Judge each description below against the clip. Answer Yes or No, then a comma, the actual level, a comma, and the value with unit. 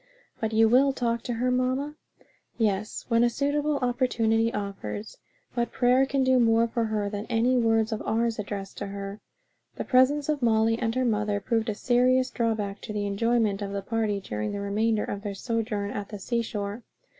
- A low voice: No, high, 225 Hz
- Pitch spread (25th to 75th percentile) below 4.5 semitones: Yes, average, 3.0 semitones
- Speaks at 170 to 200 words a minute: Yes, average, 190 wpm